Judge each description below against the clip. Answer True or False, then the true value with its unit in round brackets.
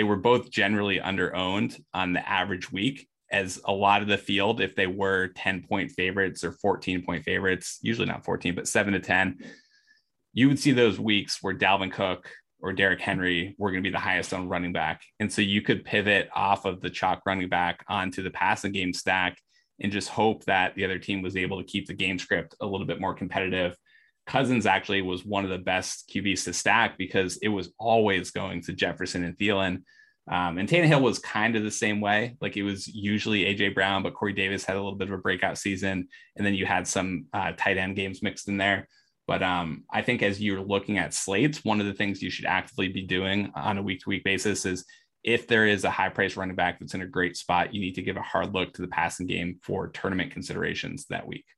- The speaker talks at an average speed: False (230 wpm)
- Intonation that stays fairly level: True (1.9 semitones)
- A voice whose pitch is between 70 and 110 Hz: True (95 Hz)